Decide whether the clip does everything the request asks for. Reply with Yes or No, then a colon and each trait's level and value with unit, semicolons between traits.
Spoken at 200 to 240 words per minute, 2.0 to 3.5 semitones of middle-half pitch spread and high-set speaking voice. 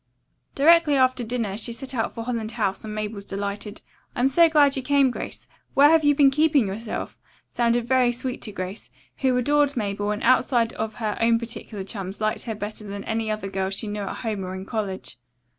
No: fast, 205 wpm; average, 3.9 semitones; high, 225 Hz